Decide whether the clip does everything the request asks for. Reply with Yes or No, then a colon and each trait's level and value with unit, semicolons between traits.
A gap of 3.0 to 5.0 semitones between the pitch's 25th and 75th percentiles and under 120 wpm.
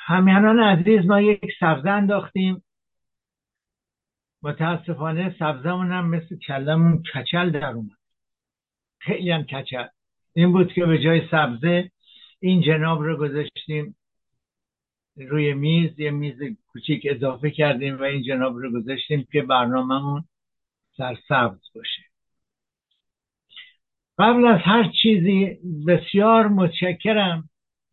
Yes: average, 4.2 semitones; slow, 105 wpm